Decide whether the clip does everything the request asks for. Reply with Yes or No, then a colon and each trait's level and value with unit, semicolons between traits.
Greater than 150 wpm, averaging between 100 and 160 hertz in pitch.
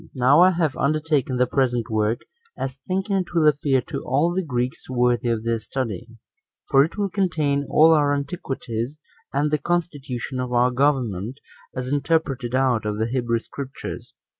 Yes: average, 175 wpm; low, 135 Hz